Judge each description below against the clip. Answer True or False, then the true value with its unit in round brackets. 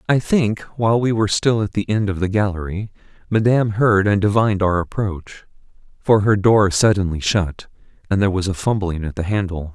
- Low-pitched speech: True (100 Hz)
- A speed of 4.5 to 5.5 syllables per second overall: True (5.4 syllables/s)